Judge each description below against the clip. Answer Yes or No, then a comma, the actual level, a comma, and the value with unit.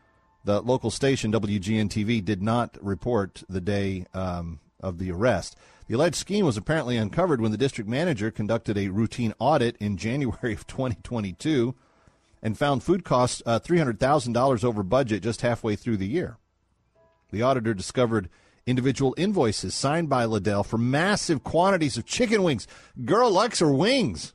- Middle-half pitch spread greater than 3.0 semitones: Yes, average, 4.2 semitones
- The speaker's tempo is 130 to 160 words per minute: Yes, average, 155 wpm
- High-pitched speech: No, low, 115 Hz